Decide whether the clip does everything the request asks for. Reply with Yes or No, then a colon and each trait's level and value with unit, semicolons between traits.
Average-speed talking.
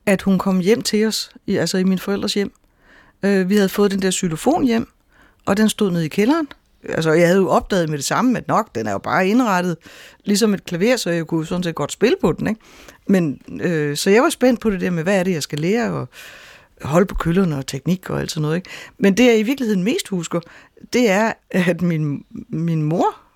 No: fast, 240 wpm